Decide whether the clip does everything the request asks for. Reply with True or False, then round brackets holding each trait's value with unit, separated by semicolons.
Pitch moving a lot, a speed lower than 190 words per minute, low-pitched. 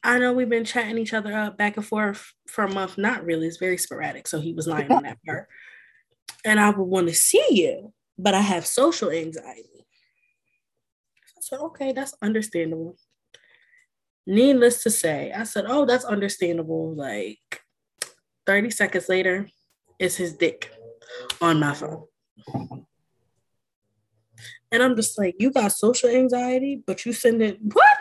False (6.8 semitones; 160 wpm; 210 Hz)